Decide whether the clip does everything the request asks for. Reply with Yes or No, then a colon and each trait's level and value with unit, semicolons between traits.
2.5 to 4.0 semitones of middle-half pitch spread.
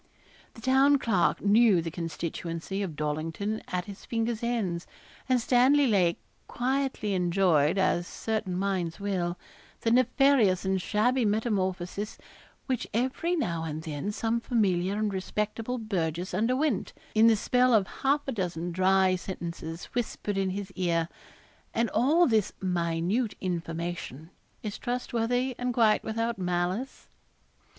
No: average, 5.1 semitones